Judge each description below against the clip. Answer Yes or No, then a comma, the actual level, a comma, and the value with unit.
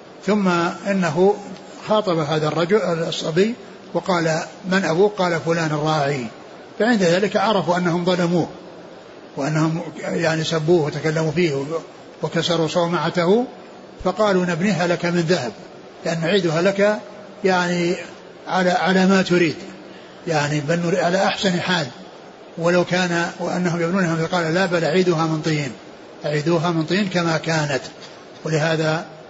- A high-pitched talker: No, medium, 175 Hz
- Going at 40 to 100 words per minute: No, average, 120 wpm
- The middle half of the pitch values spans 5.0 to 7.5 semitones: No, narrow, 2.6 semitones